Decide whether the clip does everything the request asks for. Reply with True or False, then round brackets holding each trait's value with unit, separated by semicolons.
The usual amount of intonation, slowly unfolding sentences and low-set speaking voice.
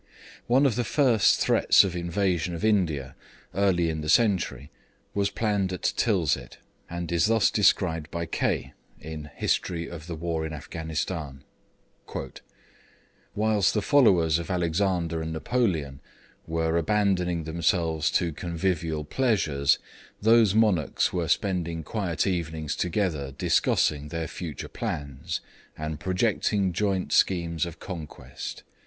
True (3.8 semitones; 125 wpm; 85 Hz)